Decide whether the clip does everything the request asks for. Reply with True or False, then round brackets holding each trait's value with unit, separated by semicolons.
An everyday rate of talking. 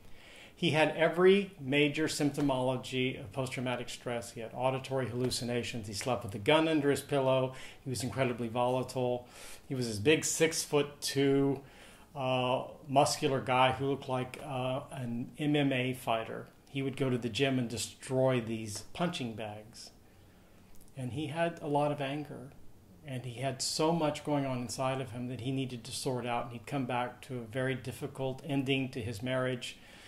True (175 wpm)